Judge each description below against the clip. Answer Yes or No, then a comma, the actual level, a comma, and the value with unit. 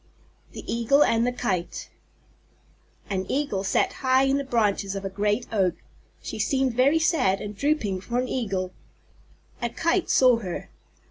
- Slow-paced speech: No, average, 160 wpm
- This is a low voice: No, high, 230 Hz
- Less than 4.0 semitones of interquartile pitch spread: No, average, 5.3 semitones